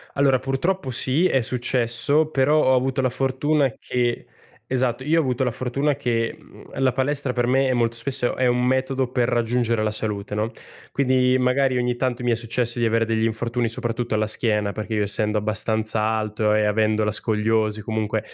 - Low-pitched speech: Yes, low, 120 Hz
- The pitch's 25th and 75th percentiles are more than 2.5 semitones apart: Yes, average, 2.9 semitones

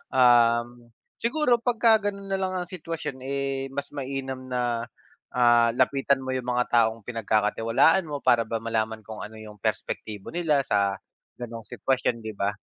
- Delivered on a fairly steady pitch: No, average, 3.7 semitones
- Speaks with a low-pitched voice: Yes, low, 125 Hz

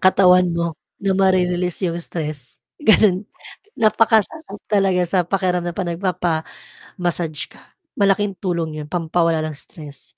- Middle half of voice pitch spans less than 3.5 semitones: Yes, average, 2.7 semitones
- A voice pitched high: No, medium, 180 Hz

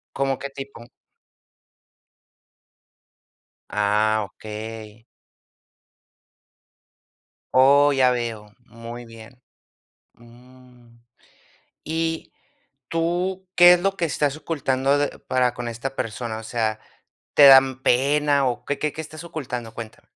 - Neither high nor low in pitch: No, low, 130 Hz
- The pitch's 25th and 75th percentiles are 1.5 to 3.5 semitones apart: No, average, 3.9 semitones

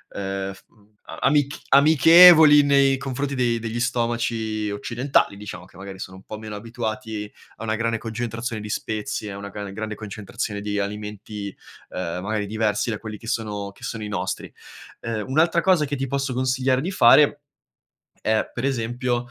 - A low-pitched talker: Yes, low, 115 Hz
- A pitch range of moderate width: Yes, average, 3.8 semitones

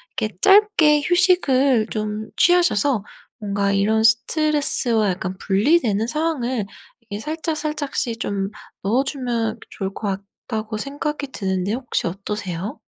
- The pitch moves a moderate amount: No, wide, 6.5 semitones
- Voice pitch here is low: No, high, 230 Hz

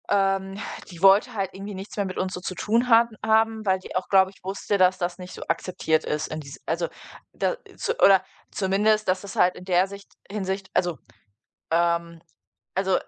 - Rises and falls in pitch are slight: Yes, narrow, 1.9 semitones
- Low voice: No, high, 190 Hz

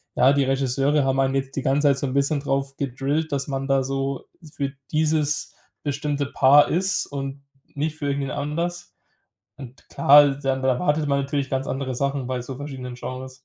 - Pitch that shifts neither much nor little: No, narrow, 1.4 semitones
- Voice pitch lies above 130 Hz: Yes, medium, 140 Hz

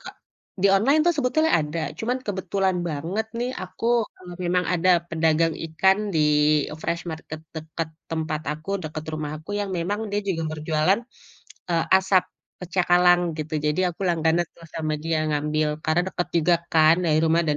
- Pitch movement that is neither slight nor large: Yes, average, 3.2 semitones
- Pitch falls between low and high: Yes, medium, 165 Hz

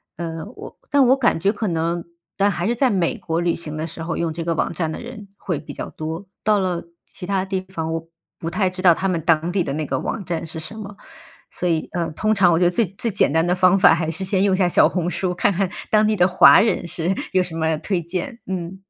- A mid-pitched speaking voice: Yes, medium, 180 Hz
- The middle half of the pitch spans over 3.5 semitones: No, average, 3.0 semitones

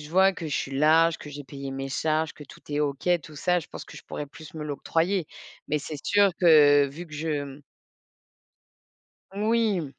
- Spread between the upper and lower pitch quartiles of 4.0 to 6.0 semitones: No, average, 2.8 semitones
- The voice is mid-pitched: Yes, medium, 155 Hz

